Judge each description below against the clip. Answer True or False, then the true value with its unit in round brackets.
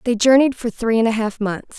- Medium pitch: False (230 Hz)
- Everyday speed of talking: False (270 wpm)